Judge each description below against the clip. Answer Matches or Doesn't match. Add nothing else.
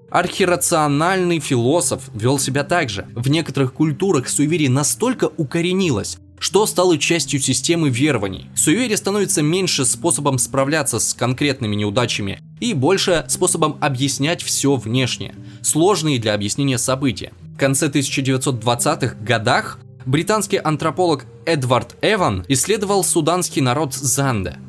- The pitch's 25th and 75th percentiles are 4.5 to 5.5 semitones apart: Matches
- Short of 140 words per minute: Matches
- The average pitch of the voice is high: Doesn't match